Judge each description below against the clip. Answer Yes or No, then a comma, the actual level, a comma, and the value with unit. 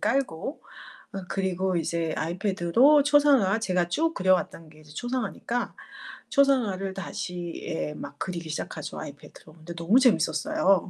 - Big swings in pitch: Yes, wide, 6.7 semitones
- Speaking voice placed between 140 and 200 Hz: Yes, high, 190 Hz